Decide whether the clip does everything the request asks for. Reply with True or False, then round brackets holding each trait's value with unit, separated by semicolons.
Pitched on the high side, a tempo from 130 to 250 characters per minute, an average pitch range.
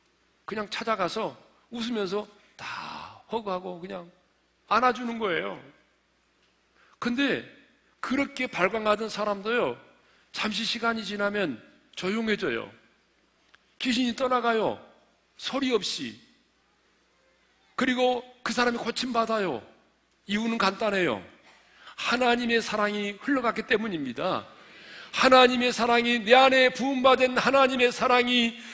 True (235 Hz; 245 characters per minute; 3.1 semitones)